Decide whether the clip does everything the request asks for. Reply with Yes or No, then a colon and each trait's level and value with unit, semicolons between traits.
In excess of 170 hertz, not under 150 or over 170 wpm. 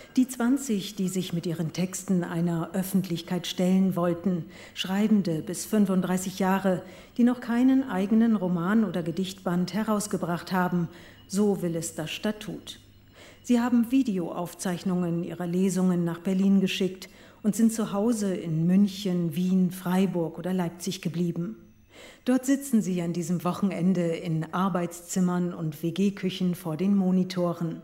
No: medium, 185 Hz; average, 130 wpm